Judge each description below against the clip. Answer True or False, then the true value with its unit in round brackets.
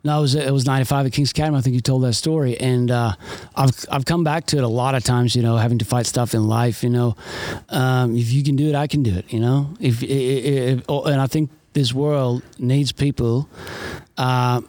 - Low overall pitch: True (130 Hz)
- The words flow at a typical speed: False (250 wpm)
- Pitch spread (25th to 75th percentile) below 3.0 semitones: True (2.6 semitones)